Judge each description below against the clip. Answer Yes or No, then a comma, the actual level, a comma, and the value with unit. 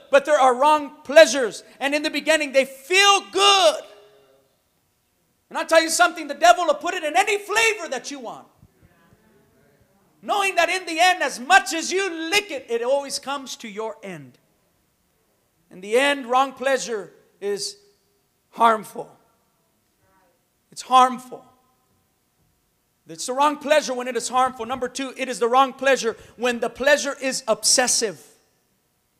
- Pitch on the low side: No, very high, 275 Hz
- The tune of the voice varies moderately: Yes, average, 4.7 semitones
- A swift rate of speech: No, average, 150 wpm